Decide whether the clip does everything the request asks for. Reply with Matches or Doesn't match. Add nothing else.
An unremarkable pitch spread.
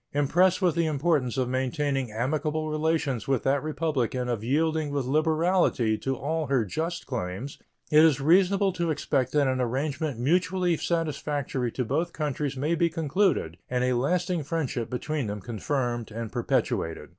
Matches